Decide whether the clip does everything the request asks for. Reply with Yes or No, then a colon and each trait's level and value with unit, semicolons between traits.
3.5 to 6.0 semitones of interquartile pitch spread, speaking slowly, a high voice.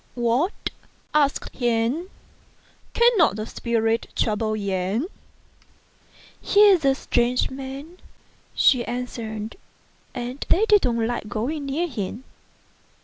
Yes: average, 4.9 semitones; slow, 125 wpm; high, 245 Hz